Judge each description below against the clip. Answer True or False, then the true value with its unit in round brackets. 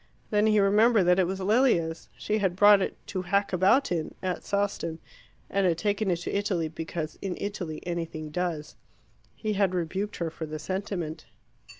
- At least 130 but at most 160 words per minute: False (180 wpm)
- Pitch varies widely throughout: False (3.4 semitones)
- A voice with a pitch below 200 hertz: True (185 Hz)